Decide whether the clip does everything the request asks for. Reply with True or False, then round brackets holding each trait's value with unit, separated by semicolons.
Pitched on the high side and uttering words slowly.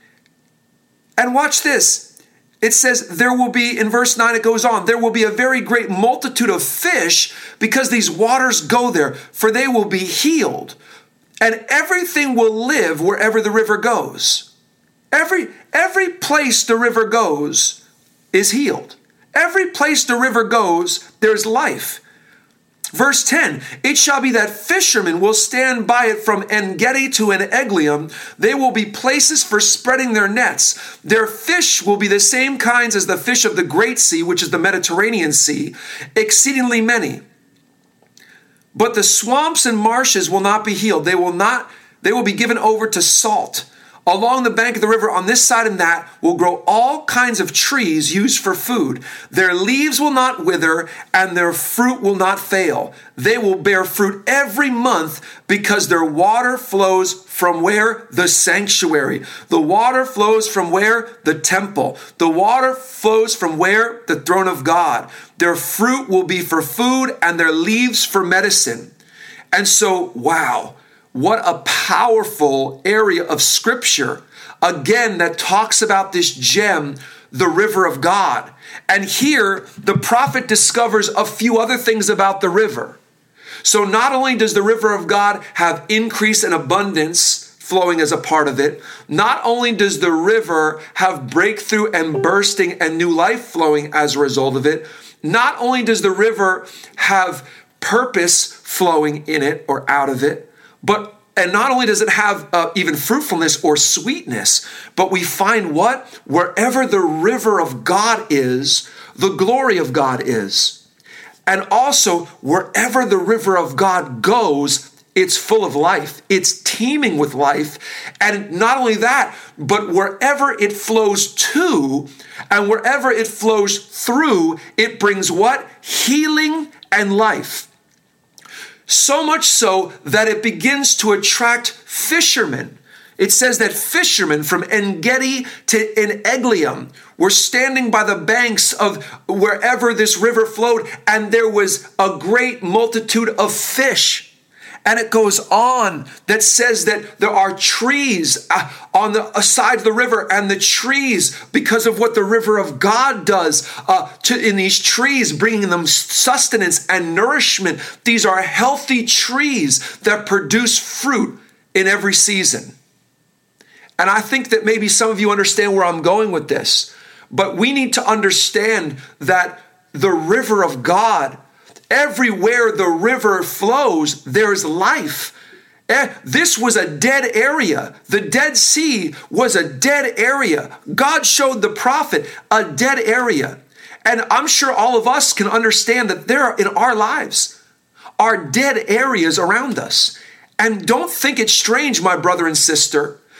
False (215 Hz; 155 wpm)